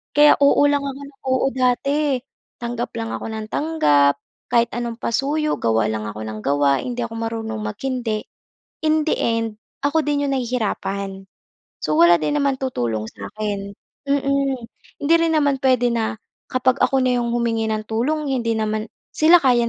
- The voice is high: Yes, high, 235 Hz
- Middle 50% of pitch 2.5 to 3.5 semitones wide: No, average, 4.5 semitones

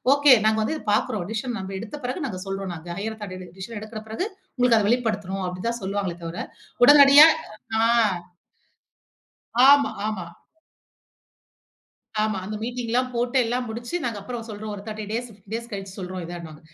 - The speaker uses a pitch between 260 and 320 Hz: No, high, 215 Hz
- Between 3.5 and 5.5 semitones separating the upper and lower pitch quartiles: Yes, average, 3.8 semitones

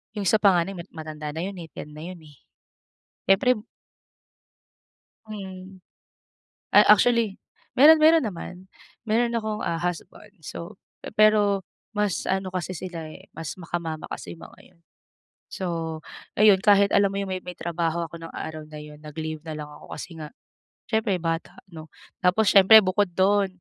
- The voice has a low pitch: No, medium, 185 Hz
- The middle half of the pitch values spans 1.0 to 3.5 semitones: No, average, 3.9 semitones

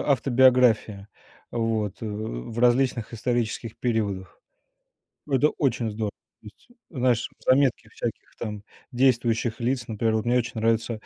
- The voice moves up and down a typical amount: No, narrow, 2.3 semitones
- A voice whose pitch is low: Yes, low, 115 Hz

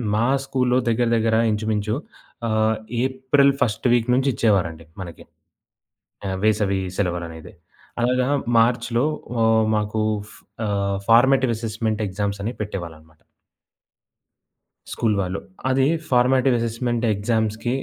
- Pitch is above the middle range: No, low, 110 Hz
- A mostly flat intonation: No, average, 3.2 semitones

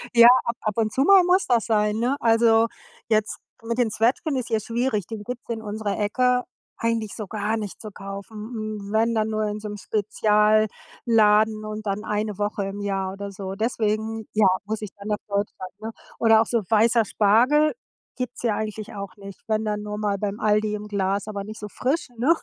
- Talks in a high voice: Yes, high, 215 Hz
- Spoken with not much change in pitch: Yes, narrow, 1.6 semitones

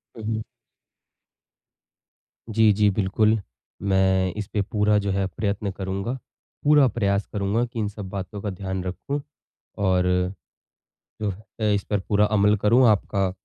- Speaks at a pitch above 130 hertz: No, low, 100 Hz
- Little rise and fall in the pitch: Yes, narrow, 2.0 semitones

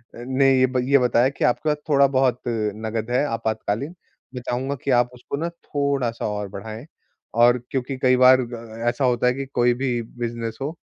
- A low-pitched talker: Yes, low, 125 Hz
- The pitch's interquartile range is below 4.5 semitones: Yes, narrow, 2.5 semitones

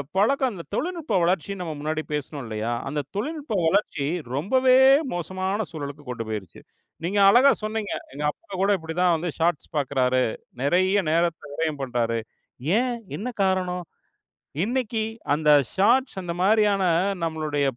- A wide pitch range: Yes, wide, 6.1 semitones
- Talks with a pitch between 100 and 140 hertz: No, medium, 175 Hz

